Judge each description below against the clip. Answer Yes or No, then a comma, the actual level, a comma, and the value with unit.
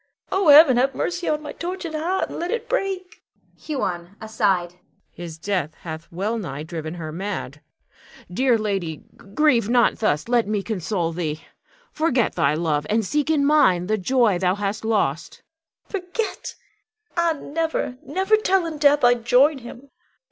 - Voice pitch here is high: Yes, high, 230 Hz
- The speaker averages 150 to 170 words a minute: Yes, average, 160 wpm